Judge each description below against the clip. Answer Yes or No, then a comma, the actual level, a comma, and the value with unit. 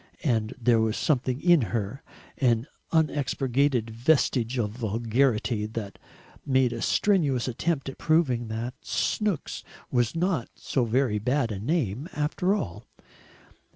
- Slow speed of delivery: Yes, slow, 125 wpm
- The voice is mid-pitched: No, low, 125 Hz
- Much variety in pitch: No, average, 4.5 semitones